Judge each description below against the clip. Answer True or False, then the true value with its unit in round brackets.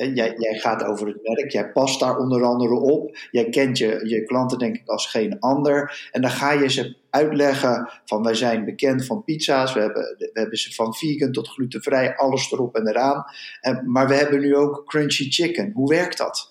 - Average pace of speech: False (215 wpm)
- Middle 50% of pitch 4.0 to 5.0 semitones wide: False (3.2 semitones)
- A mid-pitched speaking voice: False (130 Hz)